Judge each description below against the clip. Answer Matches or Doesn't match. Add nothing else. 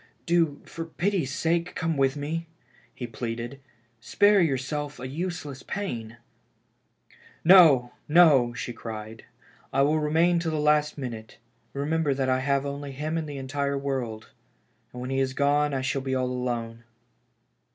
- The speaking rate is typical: Matches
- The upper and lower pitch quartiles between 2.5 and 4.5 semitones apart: Matches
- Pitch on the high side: Doesn't match